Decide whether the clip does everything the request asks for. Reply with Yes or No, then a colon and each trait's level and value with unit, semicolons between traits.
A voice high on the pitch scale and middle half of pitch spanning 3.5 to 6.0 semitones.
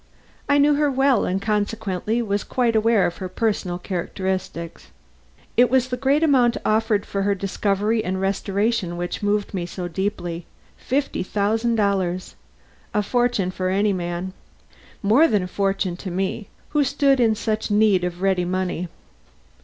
Yes: high, 205 Hz; average, 3.8 semitones